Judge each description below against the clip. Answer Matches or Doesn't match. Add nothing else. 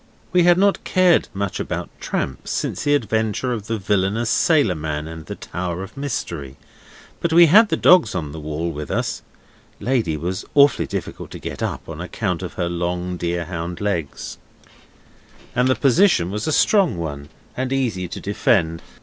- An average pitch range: Doesn't match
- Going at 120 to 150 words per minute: Doesn't match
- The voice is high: Doesn't match